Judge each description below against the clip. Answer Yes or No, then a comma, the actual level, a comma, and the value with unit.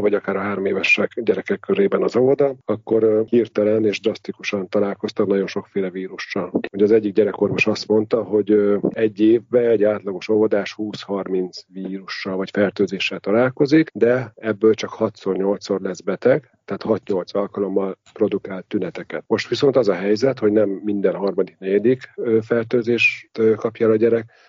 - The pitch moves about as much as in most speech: No, narrow, 2.2 semitones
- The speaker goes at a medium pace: Yes, average, 145 wpm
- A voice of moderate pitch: No, low, 105 Hz